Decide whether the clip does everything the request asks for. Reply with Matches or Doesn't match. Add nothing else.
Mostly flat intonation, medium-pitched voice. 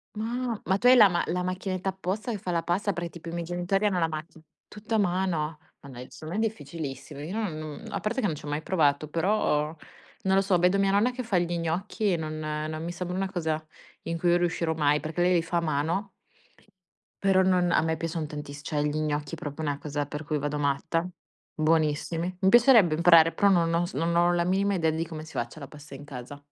Doesn't match